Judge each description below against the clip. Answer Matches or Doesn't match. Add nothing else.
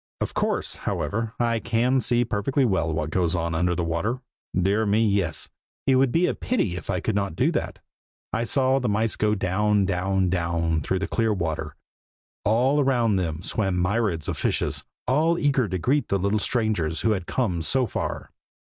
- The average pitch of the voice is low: Matches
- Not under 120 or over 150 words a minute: Doesn't match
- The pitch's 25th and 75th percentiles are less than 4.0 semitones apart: Doesn't match